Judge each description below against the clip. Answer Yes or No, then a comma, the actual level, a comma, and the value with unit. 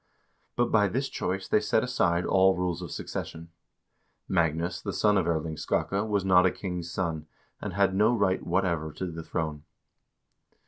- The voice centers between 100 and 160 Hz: No, very low, 90 Hz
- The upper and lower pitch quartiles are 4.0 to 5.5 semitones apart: No, average, 2.8 semitones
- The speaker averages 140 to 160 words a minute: No, average, 170 wpm